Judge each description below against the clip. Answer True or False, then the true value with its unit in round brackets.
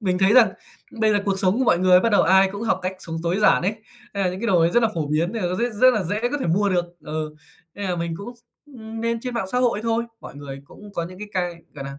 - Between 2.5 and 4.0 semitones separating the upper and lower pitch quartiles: False (4.4 semitones)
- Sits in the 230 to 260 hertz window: False (190 Hz)